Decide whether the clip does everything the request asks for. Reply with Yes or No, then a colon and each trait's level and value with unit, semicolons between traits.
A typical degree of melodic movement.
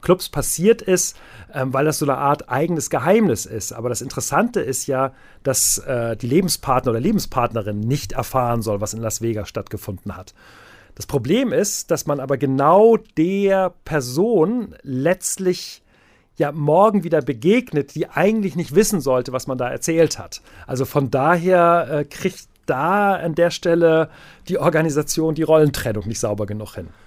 No: wide, 6.2 semitones